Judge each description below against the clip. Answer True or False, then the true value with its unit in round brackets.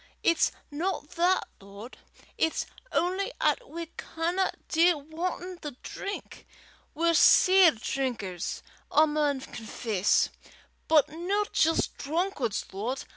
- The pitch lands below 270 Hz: False (320 Hz)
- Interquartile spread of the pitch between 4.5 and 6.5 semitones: True (5.2 semitones)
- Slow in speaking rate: True (110 wpm)